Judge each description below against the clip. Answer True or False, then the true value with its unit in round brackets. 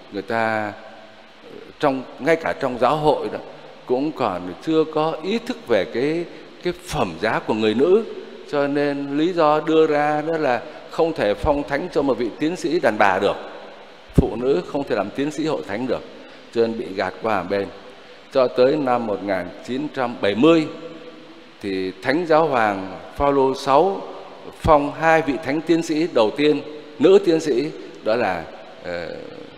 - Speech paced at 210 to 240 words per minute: False (165 wpm)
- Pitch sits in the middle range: True (150 Hz)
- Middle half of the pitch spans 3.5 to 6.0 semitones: True (5.7 semitones)